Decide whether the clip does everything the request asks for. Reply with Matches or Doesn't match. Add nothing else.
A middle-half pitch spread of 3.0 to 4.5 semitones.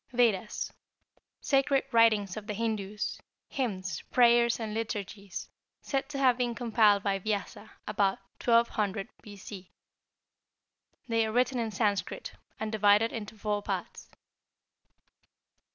Doesn't match